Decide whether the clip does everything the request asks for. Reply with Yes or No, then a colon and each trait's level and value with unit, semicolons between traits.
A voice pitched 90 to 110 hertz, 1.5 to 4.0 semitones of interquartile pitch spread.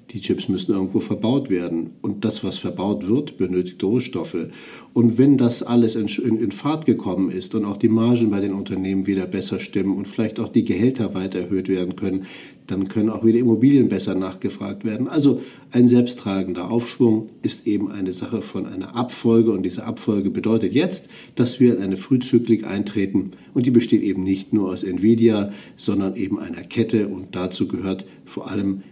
Yes: low, 105 Hz; average, 3.7 semitones